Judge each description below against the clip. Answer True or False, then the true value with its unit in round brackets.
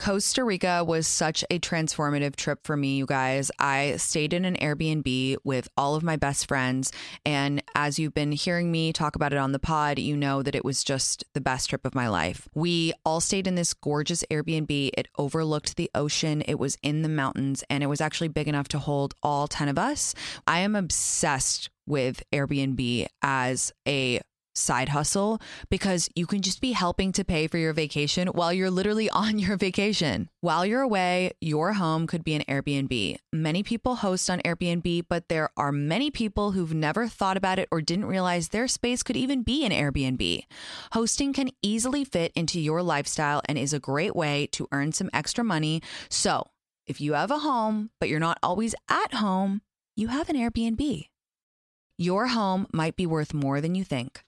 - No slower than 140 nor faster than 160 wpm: False (195 wpm)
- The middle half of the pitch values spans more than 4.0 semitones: True (4.9 semitones)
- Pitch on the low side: False (160 Hz)